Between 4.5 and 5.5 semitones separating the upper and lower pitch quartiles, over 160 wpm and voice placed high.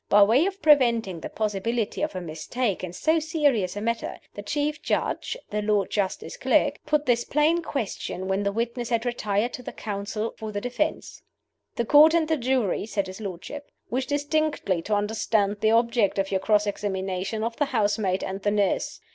Yes: average, 4.8 semitones; average, 190 wpm; high, 220 Hz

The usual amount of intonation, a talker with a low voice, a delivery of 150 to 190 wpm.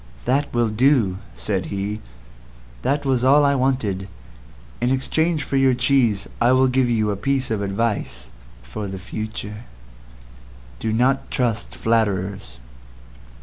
No: average, 4.6 semitones; low, 115 Hz; slow, 135 wpm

